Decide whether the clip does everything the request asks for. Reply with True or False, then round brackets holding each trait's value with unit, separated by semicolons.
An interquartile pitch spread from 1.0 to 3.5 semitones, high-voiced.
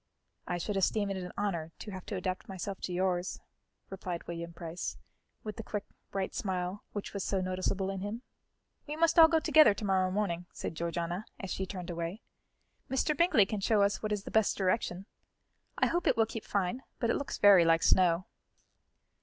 True (2.9 semitones; 195 Hz)